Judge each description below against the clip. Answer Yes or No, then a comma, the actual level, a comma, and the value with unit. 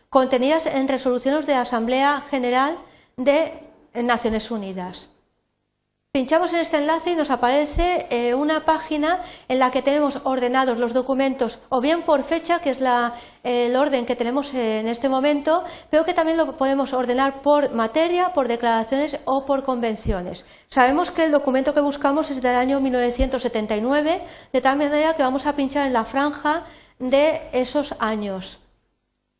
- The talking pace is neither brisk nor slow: Yes, average, 155 wpm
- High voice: Yes, very high, 275 Hz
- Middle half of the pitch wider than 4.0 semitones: No, average, 3.4 semitones